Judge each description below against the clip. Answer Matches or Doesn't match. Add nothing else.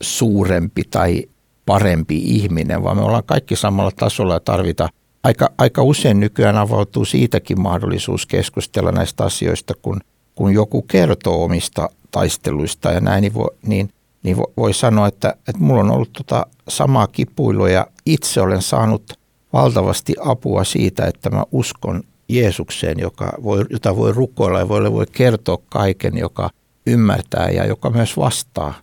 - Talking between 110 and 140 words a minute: Doesn't match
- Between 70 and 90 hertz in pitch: Doesn't match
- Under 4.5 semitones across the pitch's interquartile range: Matches